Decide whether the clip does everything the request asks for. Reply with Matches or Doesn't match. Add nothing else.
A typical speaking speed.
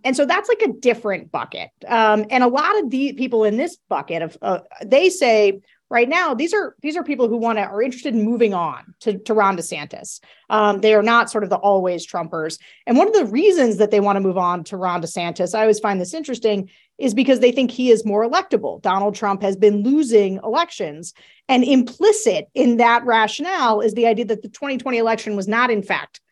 Doesn't match